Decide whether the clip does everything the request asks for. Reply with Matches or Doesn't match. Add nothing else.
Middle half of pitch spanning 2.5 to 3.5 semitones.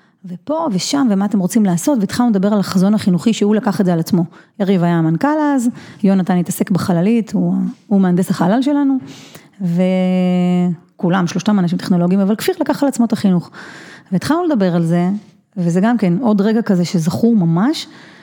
Doesn't match